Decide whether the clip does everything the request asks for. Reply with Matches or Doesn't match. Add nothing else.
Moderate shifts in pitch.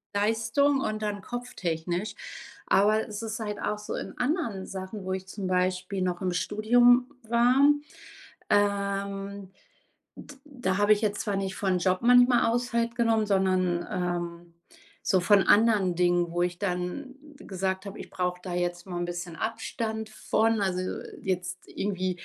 Matches